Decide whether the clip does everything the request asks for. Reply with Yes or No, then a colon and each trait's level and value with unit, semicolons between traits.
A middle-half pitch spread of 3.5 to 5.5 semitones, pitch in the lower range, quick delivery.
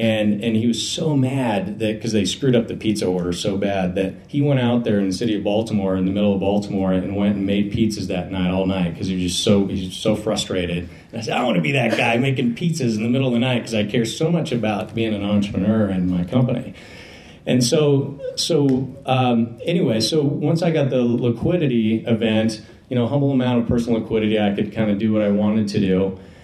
Yes: average, 3.8 semitones; low, 110 Hz; fast, 245 wpm